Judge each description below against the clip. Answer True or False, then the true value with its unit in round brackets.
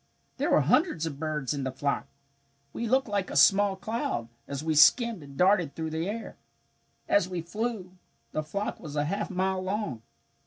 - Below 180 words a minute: False (185 wpm)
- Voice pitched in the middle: True (180 Hz)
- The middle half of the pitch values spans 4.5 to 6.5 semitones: True (5.5 semitones)